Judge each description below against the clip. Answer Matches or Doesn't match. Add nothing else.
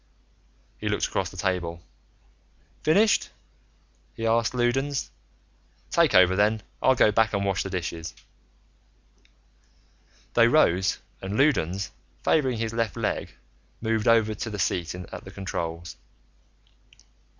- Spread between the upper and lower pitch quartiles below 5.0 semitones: Matches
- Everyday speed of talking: Doesn't match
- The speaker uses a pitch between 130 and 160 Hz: Doesn't match